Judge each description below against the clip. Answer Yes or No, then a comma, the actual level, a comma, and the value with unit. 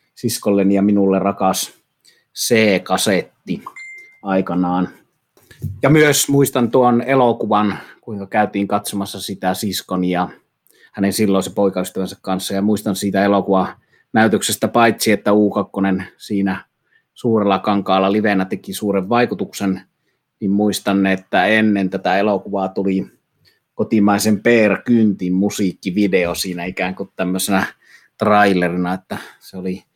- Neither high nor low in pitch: No, low, 100 Hz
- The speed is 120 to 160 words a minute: No, average, 110 wpm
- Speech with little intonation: Yes, narrow, 2.0 semitones